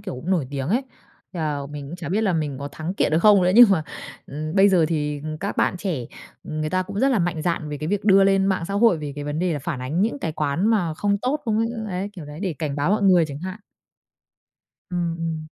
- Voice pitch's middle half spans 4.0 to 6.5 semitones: Yes, average, 4.4 semitones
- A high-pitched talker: No, medium, 170 Hz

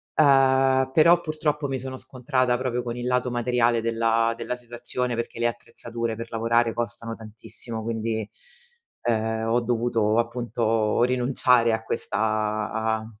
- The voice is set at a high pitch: No, low, 120 Hz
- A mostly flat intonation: Yes, narrow, 1.8 semitones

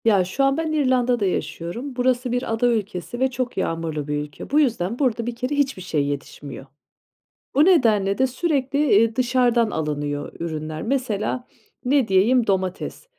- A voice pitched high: Yes, high, 235 Hz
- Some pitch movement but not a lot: No, wide, 6.4 semitones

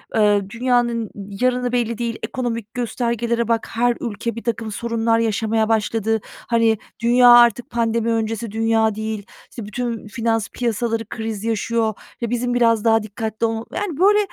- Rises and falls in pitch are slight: Yes, narrow, 1.3 semitones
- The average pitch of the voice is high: Yes, high, 230 Hz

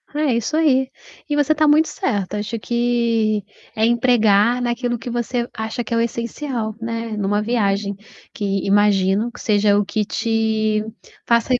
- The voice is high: Yes, high, 230 Hz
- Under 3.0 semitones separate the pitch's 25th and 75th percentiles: Yes, narrow, 2.6 semitones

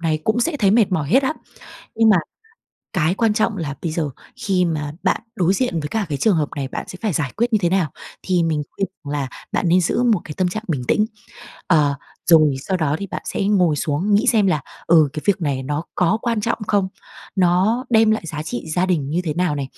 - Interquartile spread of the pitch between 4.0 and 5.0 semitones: No, wide, 5.5 semitones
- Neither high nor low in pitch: Yes, medium, 180 Hz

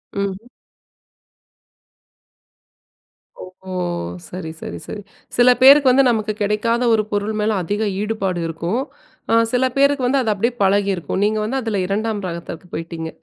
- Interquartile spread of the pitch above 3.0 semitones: Yes, average, 3.8 semitones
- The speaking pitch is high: Yes, high, 210 Hz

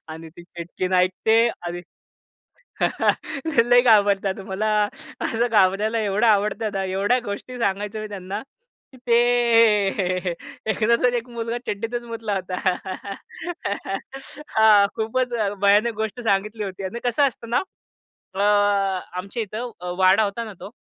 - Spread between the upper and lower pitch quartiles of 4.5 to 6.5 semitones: No, average, 3.1 semitones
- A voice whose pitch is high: Yes, high, 215 Hz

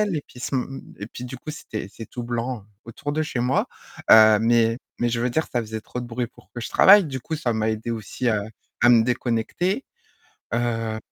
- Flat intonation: Yes, narrow, 2.2 semitones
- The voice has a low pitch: Yes, low, 120 Hz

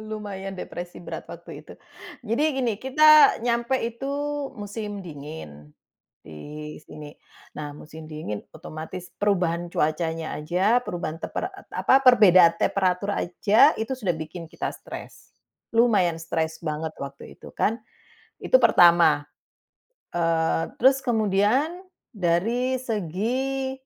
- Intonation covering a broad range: Yes, wide, 6.4 semitones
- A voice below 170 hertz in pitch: No, medium, 185 Hz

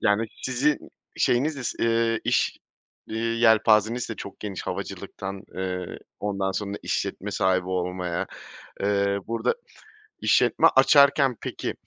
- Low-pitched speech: Yes, low, 105 Hz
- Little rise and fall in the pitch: No, average, 3.3 semitones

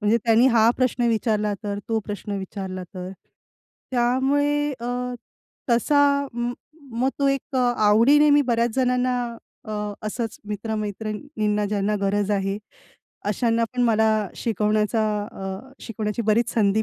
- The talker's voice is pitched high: Yes, high, 225 Hz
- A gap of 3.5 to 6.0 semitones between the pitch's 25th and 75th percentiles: No, average, 3.0 semitones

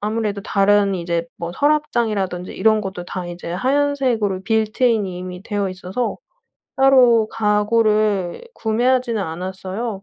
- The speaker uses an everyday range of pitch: Yes, average, 3.8 semitones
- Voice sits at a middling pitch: No, high, 210 Hz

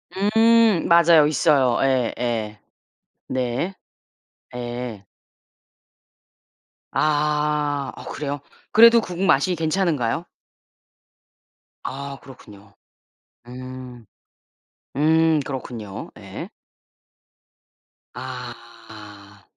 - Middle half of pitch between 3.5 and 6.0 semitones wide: Yes, average, 5.1 semitones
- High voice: No, low, 135 Hz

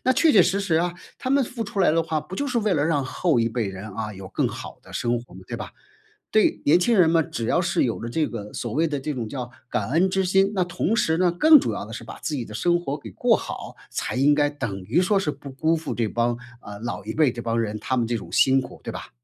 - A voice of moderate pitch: Yes, medium, 150 Hz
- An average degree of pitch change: No, wide, 7.3 semitones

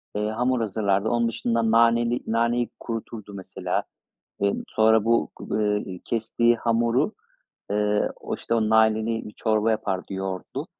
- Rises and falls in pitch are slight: Yes, narrow, 1.9 semitones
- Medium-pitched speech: No, low, 110 Hz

